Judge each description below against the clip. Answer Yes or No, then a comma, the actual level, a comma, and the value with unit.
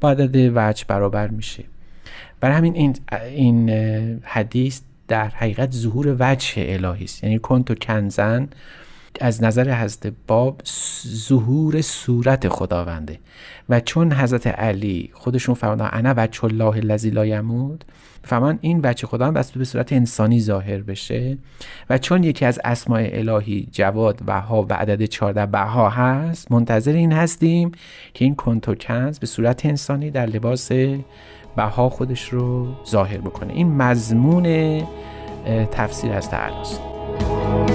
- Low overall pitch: Yes, low, 120 Hz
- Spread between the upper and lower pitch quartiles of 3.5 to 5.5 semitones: Yes, average, 3.8 semitones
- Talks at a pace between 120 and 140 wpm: Yes, average, 130 wpm